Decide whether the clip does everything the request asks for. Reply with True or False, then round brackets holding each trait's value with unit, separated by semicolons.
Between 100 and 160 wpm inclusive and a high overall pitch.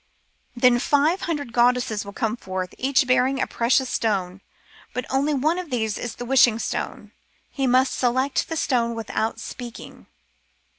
True (155 wpm; 250 Hz)